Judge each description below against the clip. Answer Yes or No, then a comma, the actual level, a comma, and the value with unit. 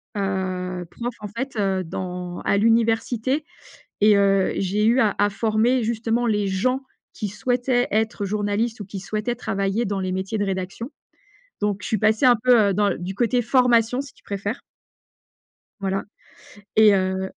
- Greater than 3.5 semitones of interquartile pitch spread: No, average, 3.2 semitones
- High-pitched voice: Yes, high, 210 Hz